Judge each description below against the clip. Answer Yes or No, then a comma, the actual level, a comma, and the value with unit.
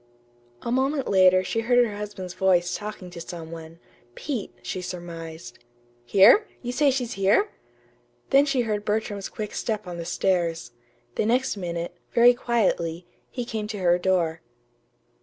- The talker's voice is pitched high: Yes, high, 195 Hz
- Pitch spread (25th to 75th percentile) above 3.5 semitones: Yes, average, 5.3 semitones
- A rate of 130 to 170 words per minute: Yes, average, 155 wpm